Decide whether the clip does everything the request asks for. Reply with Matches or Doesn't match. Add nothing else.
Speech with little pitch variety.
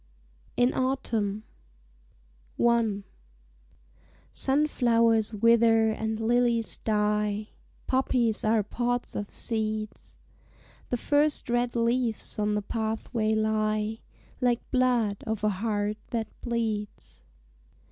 Matches